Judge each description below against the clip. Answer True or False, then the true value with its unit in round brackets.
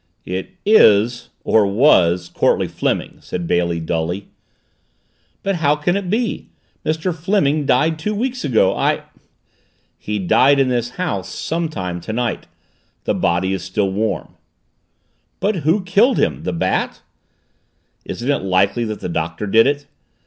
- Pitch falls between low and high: False (120 Hz)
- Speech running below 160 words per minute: True (140 wpm)